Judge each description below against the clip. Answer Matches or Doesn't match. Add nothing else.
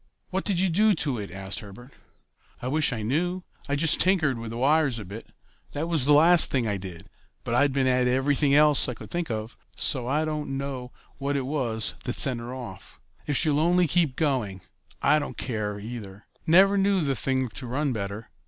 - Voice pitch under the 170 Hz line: Matches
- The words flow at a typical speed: Doesn't match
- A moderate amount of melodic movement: Matches